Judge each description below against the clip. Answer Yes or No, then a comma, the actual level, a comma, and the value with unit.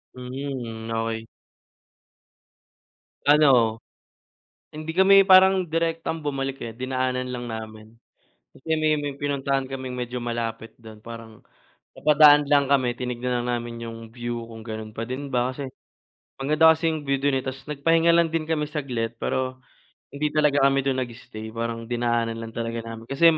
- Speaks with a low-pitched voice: Yes, low, 130 Hz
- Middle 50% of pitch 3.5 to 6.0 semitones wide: Yes, average, 4.0 semitones